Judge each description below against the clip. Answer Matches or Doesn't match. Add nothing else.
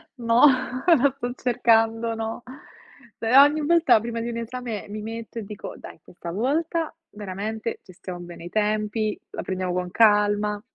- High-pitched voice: Matches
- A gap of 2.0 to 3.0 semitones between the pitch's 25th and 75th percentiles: Matches